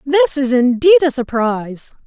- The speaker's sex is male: No, female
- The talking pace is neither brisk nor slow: Yes, average, 145 wpm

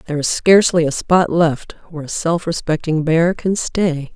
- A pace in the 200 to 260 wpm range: No, average, 190 wpm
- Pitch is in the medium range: Yes, medium, 165 Hz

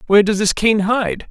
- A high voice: Yes, high, 200 Hz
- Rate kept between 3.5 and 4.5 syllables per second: No, 5.2 syllables/s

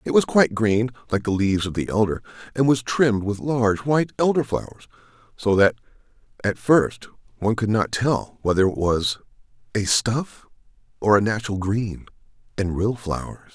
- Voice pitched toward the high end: No, low, 115 Hz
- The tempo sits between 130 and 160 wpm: No, average, 170 wpm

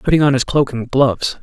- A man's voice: Yes, male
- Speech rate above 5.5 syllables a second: Yes, 6.1 syllables/s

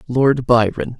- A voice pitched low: Yes, low, 125 Hz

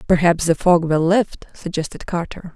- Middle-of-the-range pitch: Yes, medium, 170 Hz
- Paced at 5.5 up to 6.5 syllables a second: No, 4.7 syllables/s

